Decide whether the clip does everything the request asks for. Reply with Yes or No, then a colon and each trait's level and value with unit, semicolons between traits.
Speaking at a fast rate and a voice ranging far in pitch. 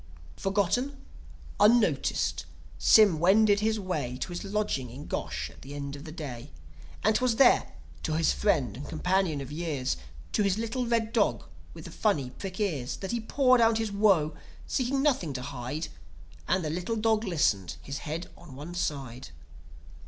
No: average, 170 wpm; wide, 7.1 semitones